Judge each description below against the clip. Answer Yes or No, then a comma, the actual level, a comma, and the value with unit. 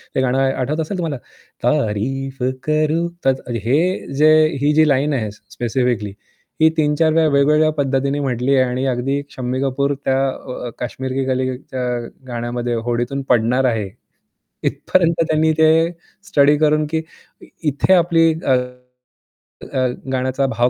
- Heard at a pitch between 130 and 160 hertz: Yes, low, 135 Hz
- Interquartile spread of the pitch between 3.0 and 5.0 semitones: Yes, average, 3.3 semitones